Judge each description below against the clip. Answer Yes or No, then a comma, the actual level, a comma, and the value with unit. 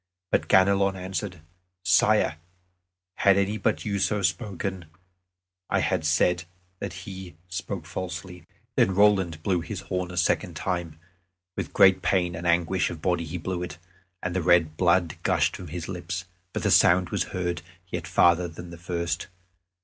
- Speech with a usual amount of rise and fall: No, narrow, 1.7 semitones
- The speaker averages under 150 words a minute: No, average, 160 wpm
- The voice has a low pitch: Yes, very low, 90 Hz